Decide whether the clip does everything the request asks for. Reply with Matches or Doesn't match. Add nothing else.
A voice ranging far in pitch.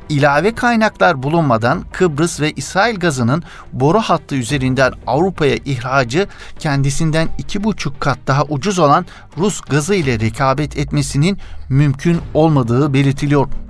Doesn't match